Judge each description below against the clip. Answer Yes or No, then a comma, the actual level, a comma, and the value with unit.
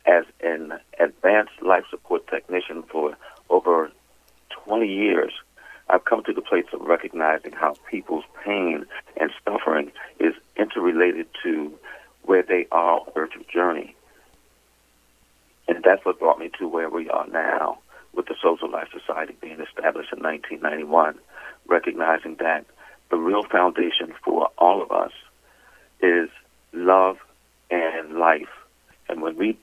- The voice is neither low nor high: No, very low, 90 Hz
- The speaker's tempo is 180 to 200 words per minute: No, slow, 135 wpm